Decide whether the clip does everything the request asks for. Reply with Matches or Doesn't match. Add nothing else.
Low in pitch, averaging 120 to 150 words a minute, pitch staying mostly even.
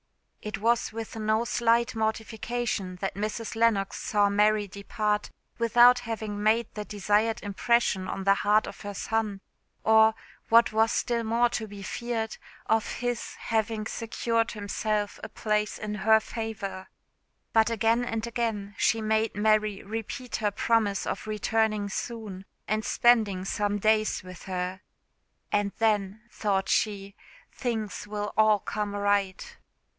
Doesn't match